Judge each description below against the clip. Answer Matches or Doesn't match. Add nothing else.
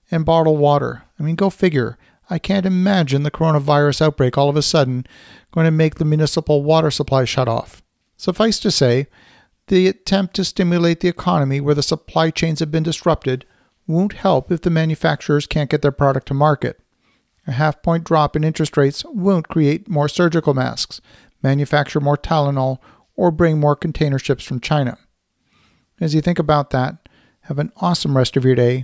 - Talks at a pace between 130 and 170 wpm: Doesn't match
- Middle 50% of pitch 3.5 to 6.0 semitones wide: Doesn't match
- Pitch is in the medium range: Matches